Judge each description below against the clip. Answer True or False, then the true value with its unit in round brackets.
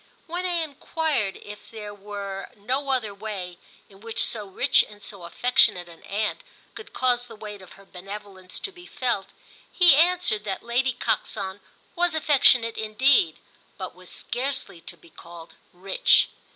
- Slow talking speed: False (155 wpm)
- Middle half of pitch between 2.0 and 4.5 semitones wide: False (5.5 semitones)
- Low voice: False (215 Hz)